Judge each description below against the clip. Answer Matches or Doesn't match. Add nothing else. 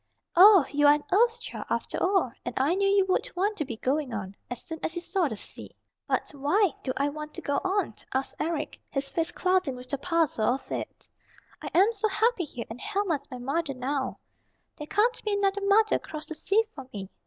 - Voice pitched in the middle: Doesn't match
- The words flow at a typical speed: Doesn't match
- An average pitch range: Doesn't match